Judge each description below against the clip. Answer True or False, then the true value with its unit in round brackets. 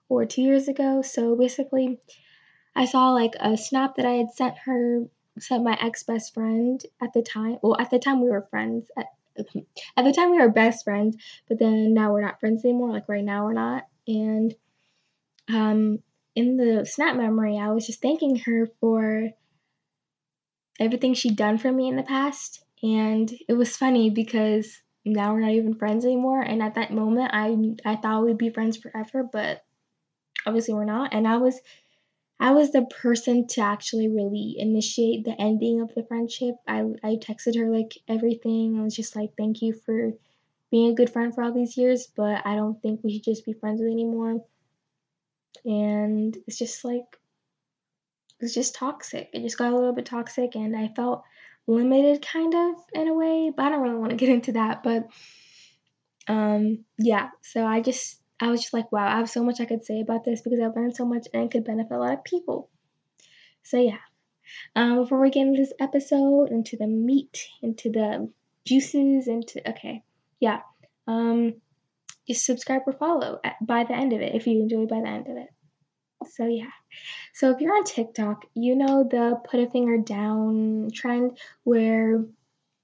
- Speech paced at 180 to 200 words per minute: True (190 wpm)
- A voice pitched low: False (230 Hz)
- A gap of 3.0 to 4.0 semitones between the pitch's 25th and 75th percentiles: False (2.4 semitones)